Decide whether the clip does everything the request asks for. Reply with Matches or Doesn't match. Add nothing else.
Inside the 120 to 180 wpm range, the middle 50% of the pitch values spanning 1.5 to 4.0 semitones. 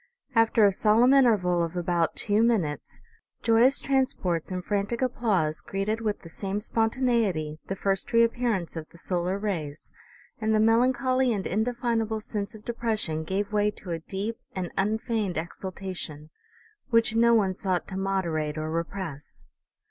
Doesn't match